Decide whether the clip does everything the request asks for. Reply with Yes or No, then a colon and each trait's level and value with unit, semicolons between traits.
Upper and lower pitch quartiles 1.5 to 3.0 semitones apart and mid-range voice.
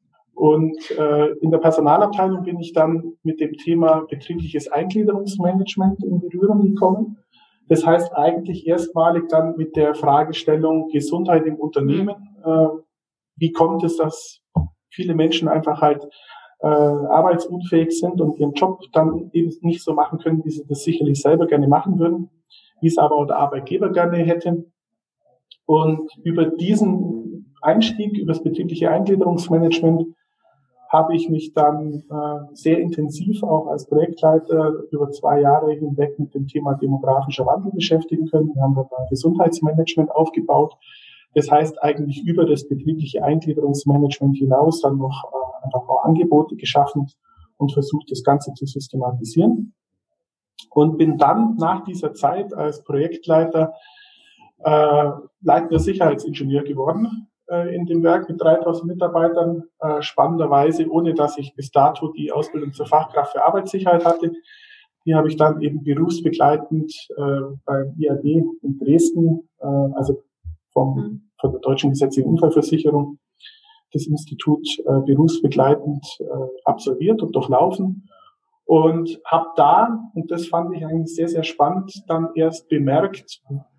Yes: narrow, 2.5 semitones; medium, 160 Hz